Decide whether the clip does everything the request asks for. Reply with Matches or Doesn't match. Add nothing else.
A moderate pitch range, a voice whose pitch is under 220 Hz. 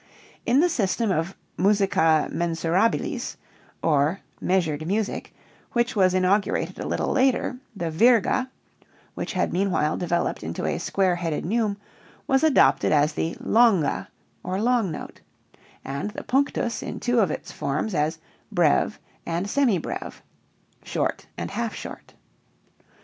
Doesn't match